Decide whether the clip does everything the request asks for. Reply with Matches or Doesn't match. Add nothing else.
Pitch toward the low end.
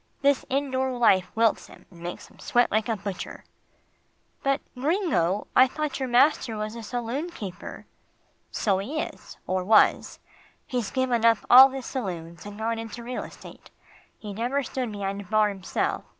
Doesn't match